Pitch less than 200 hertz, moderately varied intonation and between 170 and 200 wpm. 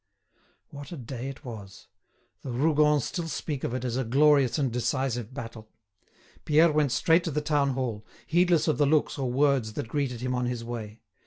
Yes: low, 135 Hz; average, 3.7 semitones; average, 195 wpm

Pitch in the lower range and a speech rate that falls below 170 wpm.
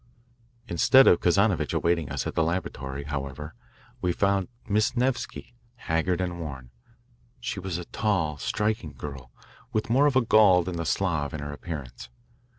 Yes: very low, 85 Hz; average, 155 wpm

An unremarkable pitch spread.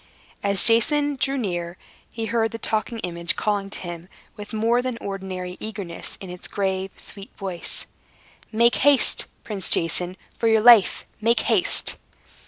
Yes: average, 3.9 semitones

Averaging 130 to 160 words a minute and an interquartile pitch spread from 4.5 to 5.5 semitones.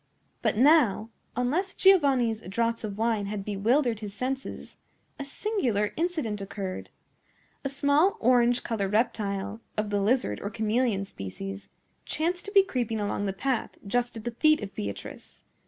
Yes: average, 150 wpm; average, 5.1 semitones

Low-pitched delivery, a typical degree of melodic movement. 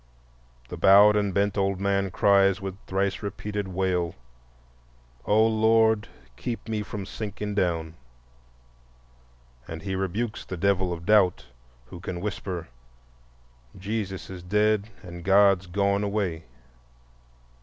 No: low, 100 Hz; narrow, 2.1 semitones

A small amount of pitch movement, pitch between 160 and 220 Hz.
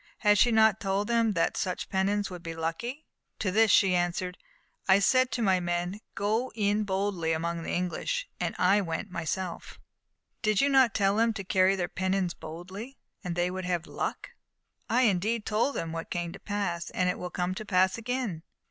No: average, 3.5 semitones; high, 190 Hz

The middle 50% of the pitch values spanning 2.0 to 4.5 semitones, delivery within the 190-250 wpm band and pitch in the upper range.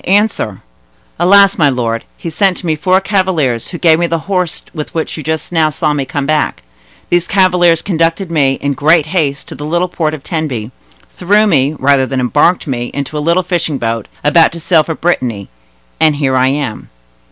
No: average, 4.1 semitones; average, 200 wpm; medium, 155 Hz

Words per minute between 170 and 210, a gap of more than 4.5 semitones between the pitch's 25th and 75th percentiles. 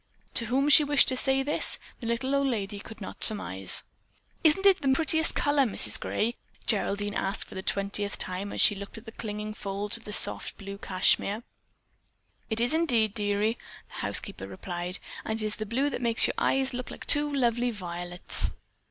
Yes: average, 185 wpm; average, 4.9 semitones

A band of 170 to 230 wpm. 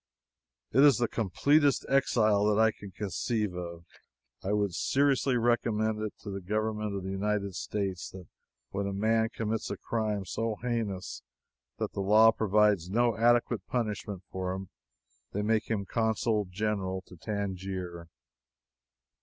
No: average, 145 wpm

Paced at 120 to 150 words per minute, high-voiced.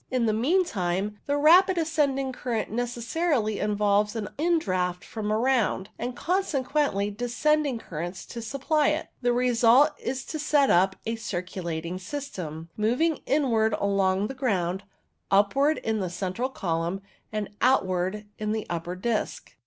Yes: average, 145 wpm; high, 225 Hz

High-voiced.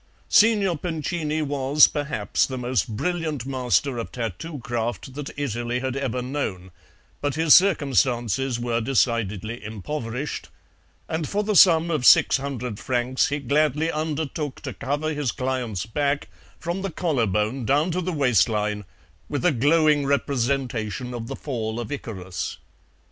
No: low, 135 Hz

